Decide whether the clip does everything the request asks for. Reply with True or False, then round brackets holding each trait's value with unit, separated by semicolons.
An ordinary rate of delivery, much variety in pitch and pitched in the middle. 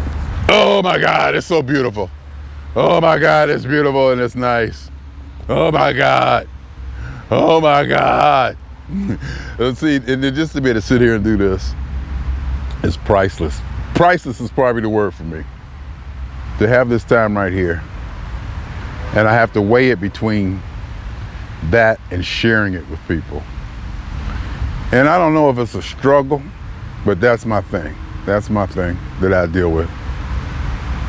False (155 wpm; 8.5 semitones; 95 Hz)